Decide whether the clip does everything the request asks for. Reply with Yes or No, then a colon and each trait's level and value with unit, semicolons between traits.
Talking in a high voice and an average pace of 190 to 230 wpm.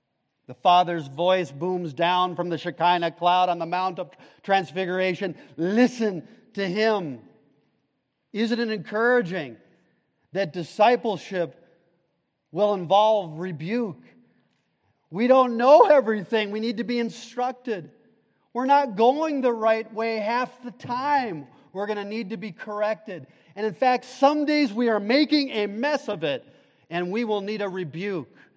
No: high, 210 Hz; average, 145 wpm